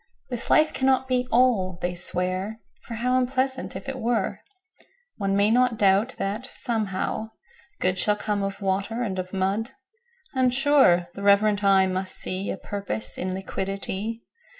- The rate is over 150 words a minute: No, slow, 135 wpm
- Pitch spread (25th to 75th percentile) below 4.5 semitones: No, average, 4.8 semitones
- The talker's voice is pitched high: Yes, high, 215 Hz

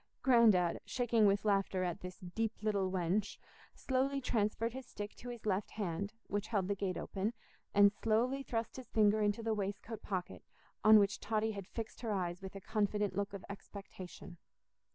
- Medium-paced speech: Yes, average, 175 wpm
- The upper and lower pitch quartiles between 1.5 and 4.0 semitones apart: Yes, narrow, 2.5 semitones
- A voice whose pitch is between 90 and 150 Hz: No, high, 205 Hz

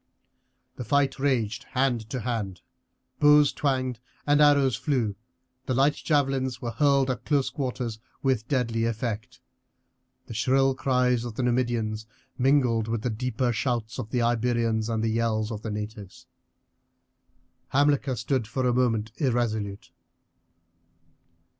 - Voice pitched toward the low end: Yes, low, 120 Hz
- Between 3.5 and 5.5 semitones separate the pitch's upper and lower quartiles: No, average, 3.0 semitones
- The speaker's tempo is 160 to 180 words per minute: No, slow, 135 wpm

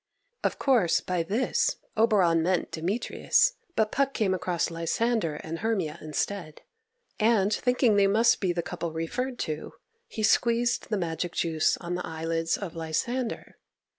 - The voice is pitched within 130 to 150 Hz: No, medium, 185 Hz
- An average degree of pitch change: No, wide, 5.7 semitones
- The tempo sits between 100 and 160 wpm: Yes, average, 145 wpm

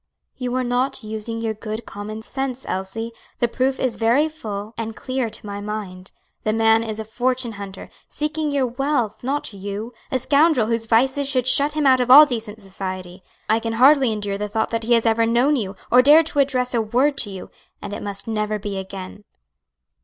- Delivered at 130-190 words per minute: No, fast, 205 wpm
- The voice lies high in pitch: Yes, high, 230 Hz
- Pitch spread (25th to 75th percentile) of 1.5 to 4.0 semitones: Yes, average, 3.6 semitones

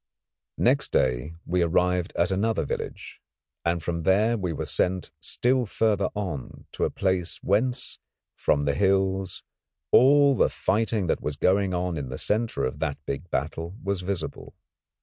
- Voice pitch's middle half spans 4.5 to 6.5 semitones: No, average, 3.7 semitones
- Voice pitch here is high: No, very low, 90 Hz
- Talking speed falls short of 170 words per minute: Yes, average, 155 wpm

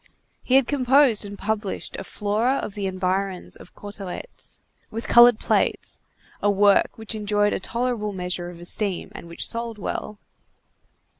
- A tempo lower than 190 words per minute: Yes, average, 150 wpm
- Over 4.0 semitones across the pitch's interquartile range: No, average, 3.2 semitones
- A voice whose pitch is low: No, high, 205 Hz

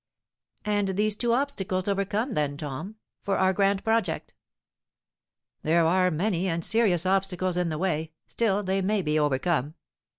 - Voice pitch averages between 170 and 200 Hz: Yes, high, 190 Hz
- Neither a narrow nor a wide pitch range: Yes, average, 3.6 semitones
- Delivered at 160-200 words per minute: No, average, 145 wpm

